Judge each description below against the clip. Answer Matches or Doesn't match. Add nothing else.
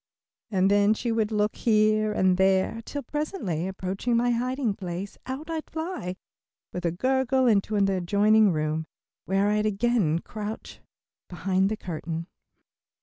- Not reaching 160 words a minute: Matches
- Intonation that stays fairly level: Doesn't match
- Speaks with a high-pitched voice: Matches